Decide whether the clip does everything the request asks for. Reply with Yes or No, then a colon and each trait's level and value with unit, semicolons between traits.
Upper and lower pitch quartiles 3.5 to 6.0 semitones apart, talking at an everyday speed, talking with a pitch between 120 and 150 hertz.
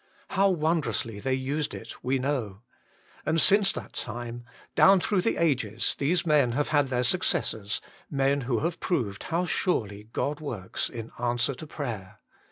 Yes: average, 5.1 semitones; average, 160 wpm; low, 135 Hz